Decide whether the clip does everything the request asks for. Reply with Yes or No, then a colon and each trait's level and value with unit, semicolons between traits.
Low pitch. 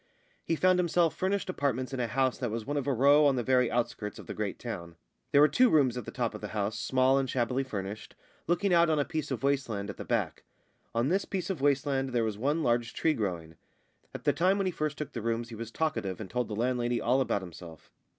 Yes: low, 130 Hz